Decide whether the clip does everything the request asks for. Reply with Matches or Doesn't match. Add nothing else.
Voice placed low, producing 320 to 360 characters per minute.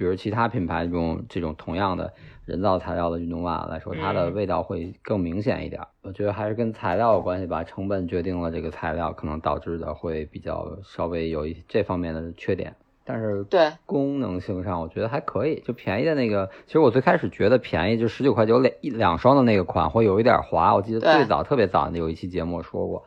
Matches